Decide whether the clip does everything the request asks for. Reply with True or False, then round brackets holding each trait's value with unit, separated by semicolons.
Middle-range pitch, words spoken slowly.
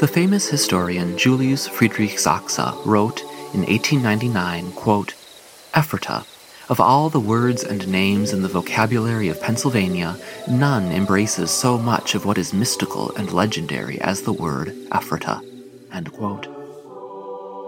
False (105 Hz; 120 wpm)